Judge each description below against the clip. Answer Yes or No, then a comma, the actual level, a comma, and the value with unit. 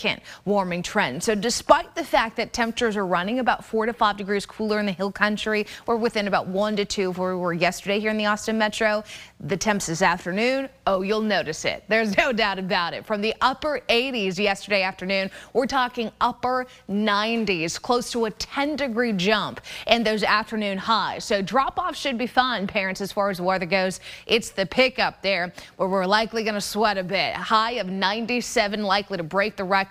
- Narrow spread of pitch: No, average, 3.0 semitones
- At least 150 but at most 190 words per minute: No, fast, 205 wpm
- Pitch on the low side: No, high, 210 Hz